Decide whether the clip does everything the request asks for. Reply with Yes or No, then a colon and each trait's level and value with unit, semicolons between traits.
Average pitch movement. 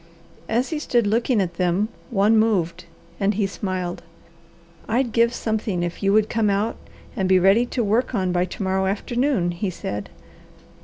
Yes: average, 3.5 semitones